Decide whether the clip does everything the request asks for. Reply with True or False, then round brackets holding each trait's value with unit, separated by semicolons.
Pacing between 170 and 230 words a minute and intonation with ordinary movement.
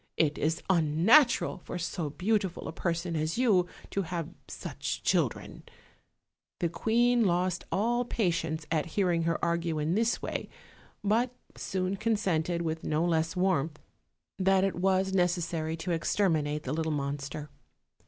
False (140 wpm; 3.3 semitones)